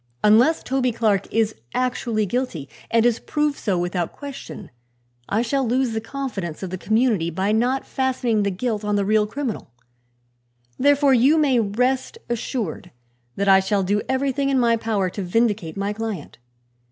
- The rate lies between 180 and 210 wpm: No, average, 165 wpm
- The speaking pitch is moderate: No, high, 225 Hz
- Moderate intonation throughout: Yes, average, 4.4 semitones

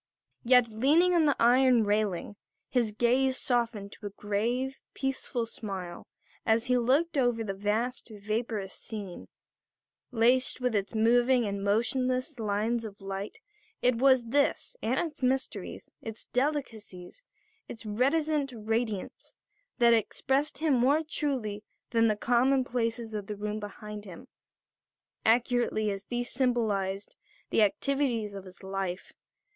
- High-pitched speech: Yes, high, 230 Hz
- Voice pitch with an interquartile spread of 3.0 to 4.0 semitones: Yes, average, 3.6 semitones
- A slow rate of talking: Yes, slow, 130 wpm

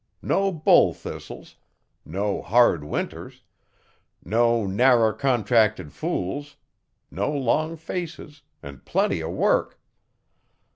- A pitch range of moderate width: No, wide, 6.5 semitones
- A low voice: Yes, low, 120 Hz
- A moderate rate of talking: No, slow, 95 wpm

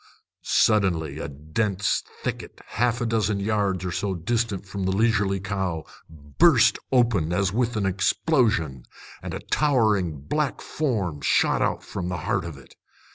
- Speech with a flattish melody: No, average, 4.8 semitones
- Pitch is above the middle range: No, low, 100 Hz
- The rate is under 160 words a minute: Yes, average, 150 wpm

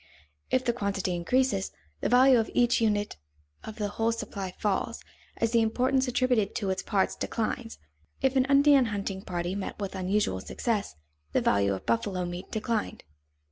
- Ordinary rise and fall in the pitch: Yes, average, 4.3 semitones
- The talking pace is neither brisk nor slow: Yes, average, 165 wpm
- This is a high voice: Yes, high, 215 Hz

